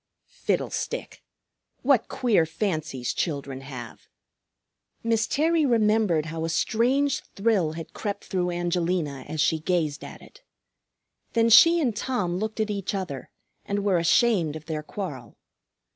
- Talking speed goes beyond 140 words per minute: No, slow, 135 wpm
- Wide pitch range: Yes, wide, 6.0 semitones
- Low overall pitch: No, medium, 185 Hz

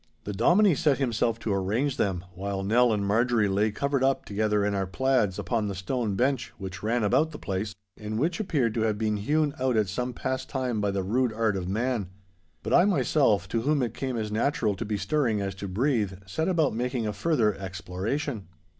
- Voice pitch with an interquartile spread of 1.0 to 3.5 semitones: No, average, 4.6 semitones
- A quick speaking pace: Yes, fast, 210 wpm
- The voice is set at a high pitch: No, low, 110 Hz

